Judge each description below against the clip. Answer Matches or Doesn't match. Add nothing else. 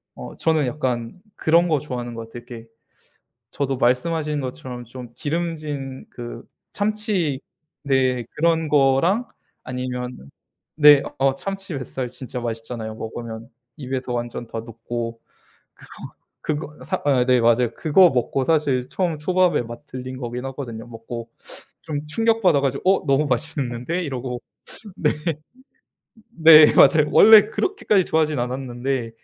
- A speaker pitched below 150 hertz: Matches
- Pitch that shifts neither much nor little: Matches